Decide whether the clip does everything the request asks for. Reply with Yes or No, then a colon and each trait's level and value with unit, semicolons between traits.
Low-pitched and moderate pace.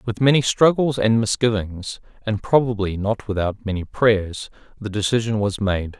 Yes: low, 110 Hz; average, 150 wpm